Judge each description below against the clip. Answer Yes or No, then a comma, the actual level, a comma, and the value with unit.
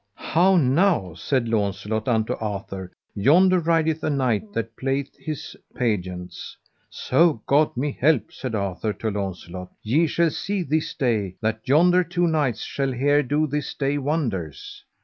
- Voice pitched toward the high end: No, low, 130 Hz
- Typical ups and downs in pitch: No, wide, 6.6 semitones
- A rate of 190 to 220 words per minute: No, average, 150 wpm